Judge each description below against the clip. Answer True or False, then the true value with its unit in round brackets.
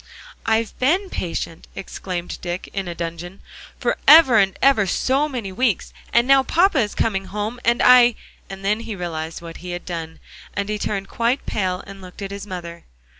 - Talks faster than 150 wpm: True (180 wpm)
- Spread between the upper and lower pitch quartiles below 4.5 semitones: False (5.0 semitones)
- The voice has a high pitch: True (200 Hz)